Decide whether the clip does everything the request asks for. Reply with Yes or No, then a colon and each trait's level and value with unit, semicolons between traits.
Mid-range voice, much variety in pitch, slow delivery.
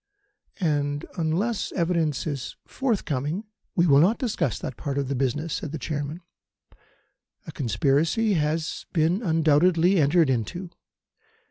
No: medium, 160 Hz; average, 3.8 semitones; slow, 130 wpm